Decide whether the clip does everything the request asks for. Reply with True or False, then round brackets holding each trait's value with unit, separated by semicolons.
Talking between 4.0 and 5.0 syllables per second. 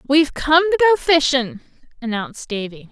False (5.6 syllables/s)